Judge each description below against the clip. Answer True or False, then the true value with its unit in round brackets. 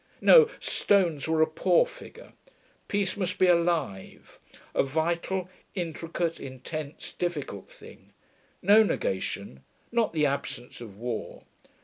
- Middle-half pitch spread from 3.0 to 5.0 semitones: False (5.4 semitones)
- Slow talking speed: True (115 wpm)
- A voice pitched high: False (165 Hz)